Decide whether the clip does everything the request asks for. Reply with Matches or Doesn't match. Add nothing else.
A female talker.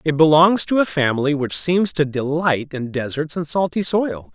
Doesn't match